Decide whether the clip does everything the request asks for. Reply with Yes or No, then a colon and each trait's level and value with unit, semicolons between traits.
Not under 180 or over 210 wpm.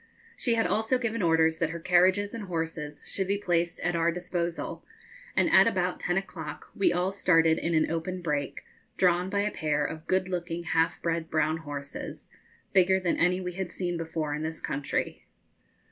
Yes: average, 185 wpm